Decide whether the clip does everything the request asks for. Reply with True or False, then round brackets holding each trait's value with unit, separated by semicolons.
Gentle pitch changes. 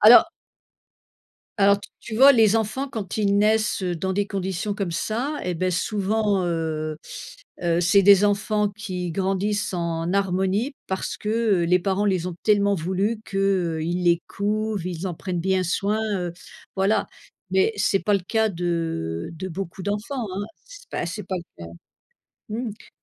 False (3.0 semitones)